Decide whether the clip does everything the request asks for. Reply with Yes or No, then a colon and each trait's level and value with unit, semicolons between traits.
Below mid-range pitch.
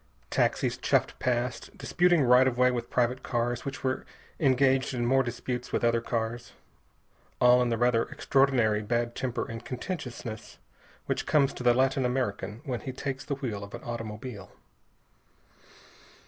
Yes: low, 125 Hz